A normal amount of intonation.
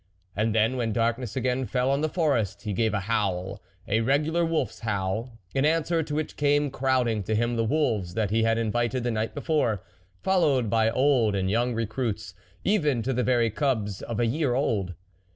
Yes: average, 3.9 semitones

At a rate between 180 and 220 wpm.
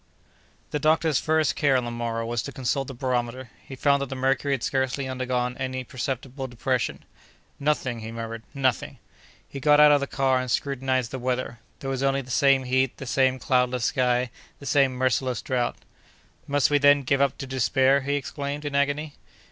Yes: average, 190 wpm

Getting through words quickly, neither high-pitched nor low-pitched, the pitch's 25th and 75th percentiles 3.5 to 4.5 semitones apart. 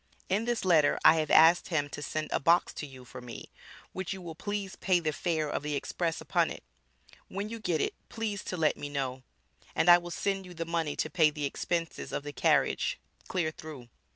Yes: fast, 220 wpm; medium, 165 Hz; average, 3.8 semitones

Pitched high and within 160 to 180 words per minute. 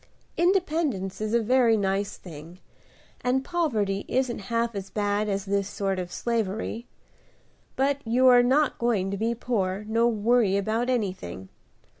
No: high, 220 Hz; average, 145 wpm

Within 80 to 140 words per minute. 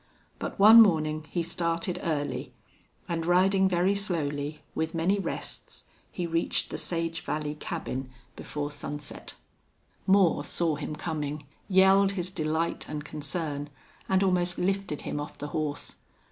Yes: slow, 135 wpm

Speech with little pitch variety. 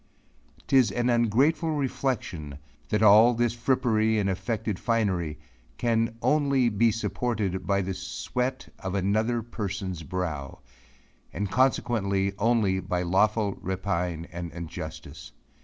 No: average, 4.2 semitones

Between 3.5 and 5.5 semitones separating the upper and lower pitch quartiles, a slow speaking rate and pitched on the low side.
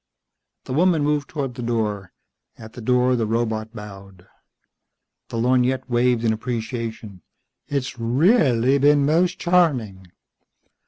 Yes: average, 4.1 semitones; slow, 120 wpm; low, 125 Hz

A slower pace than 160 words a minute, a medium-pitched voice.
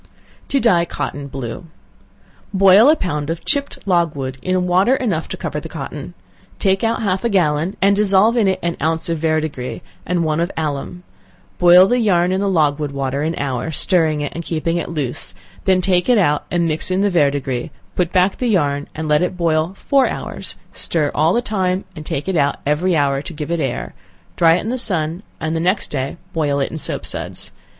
No: fast, 205 wpm; medium, 170 Hz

